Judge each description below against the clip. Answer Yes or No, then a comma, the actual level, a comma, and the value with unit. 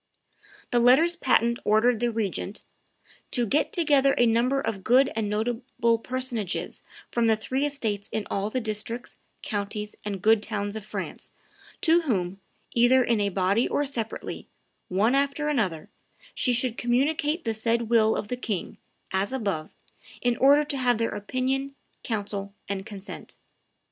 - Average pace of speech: Yes, average, 155 wpm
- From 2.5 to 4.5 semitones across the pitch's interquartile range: Yes, average, 3.8 semitones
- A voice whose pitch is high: Yes, high, 230 Hz